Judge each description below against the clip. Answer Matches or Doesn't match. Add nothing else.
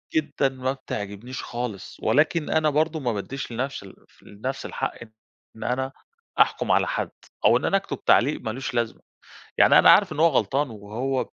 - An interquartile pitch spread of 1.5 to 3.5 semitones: Doesn't match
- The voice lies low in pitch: Matches